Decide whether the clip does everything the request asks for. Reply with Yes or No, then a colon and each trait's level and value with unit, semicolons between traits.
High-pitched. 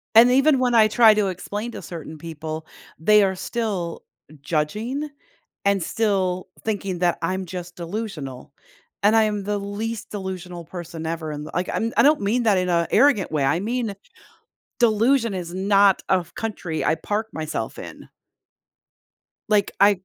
Yes: high, 195 Hz